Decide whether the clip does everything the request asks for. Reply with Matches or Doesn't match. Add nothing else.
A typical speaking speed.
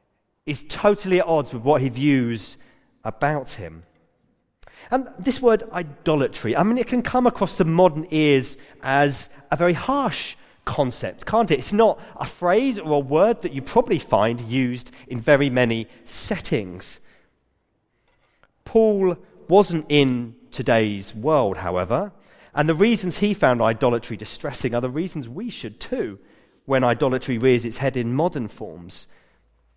Matches